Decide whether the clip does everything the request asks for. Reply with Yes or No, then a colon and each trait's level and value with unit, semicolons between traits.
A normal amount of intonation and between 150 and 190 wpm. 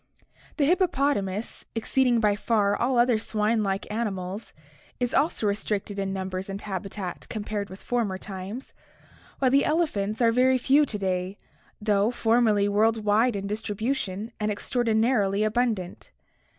No: average, 3.4 semitones; slow, 135 wpm